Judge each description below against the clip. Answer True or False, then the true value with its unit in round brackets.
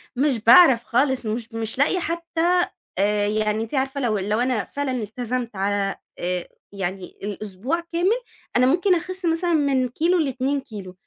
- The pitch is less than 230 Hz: False (255 Hz)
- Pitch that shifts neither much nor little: False (7.2 semitones)